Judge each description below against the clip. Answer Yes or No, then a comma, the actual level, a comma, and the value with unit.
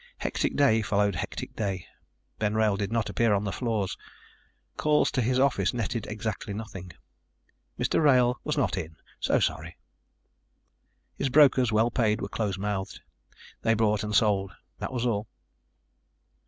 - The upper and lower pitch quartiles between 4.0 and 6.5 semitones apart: No, average, 3.1 semitones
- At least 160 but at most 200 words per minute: No, average, 150 wpm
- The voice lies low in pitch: Yes, low, 110 Hz